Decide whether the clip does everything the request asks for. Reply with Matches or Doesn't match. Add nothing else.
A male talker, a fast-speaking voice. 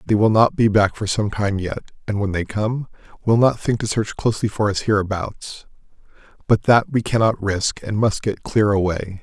Matches